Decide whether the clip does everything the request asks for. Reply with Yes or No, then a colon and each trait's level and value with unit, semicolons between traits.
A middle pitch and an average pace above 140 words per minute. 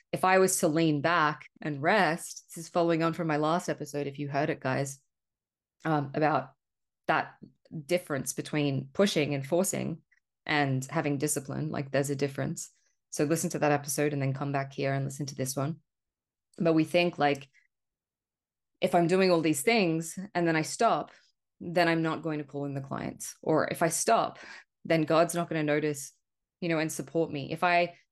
Yes: medium, 155 Hz; average, 195 wpm